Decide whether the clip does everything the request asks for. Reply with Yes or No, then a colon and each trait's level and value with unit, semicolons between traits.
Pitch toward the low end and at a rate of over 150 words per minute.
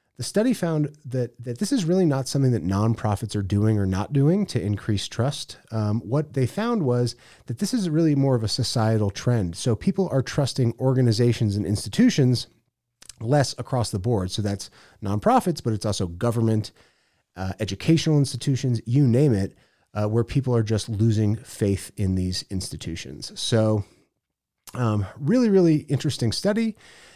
Yes: low, 120 Hz; average, 165 wpm